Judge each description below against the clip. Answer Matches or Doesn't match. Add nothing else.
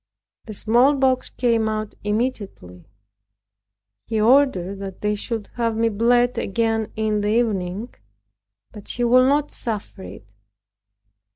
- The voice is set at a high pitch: Matches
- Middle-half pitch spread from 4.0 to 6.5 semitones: Doesn't match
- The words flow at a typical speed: Doesn't match